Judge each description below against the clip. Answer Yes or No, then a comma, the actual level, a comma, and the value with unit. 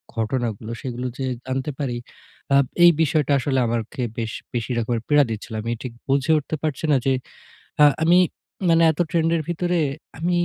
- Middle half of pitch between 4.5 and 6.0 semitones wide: Yes, average, 5.1 semitones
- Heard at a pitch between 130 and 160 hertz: Yes, low, 135 Hz